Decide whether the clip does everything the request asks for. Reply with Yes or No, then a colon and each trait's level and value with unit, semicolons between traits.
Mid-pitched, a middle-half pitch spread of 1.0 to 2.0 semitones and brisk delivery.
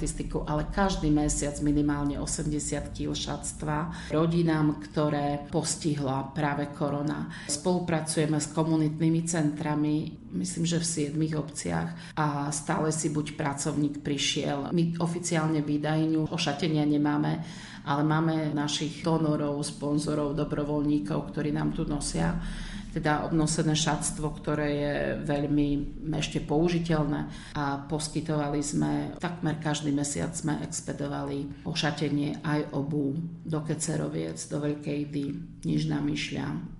No: medium, 150 Hz; narrow, 1.4 semitones; average, 115 wpm